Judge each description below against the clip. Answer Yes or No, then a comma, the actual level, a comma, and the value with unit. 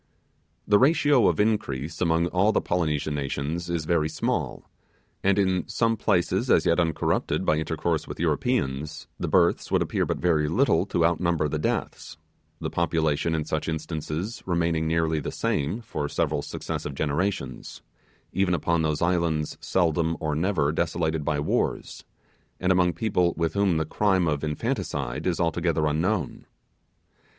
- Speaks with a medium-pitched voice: No, very low, 80 Hz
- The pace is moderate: Yes, average, 150 wpm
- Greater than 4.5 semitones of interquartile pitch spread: No, narrow, 2.6 semitones